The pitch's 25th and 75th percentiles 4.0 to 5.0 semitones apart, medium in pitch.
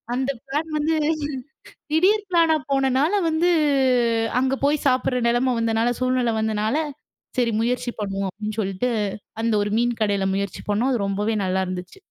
No: average, 4.5 semitones; high, 240 Hz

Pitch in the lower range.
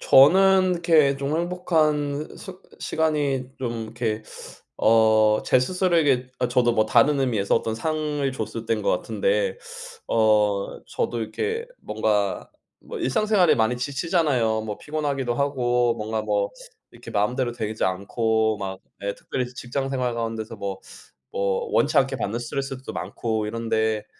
Yes: low, 125 Hz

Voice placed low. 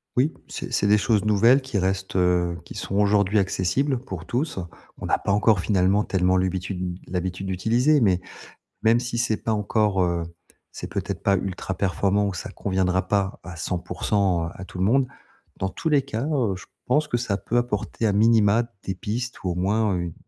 Yes: low, 100 Hz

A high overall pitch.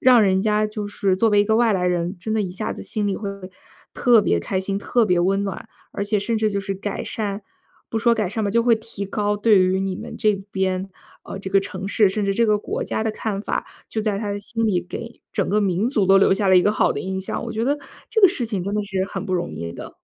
Yes: high, 205 Hz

